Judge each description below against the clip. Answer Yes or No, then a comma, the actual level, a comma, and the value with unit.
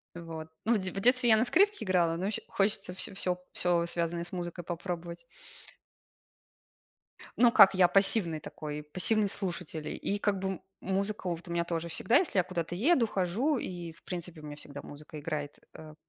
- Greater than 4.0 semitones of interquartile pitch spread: No, average, 3.2 semitones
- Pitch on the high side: No, medium, 180 Hz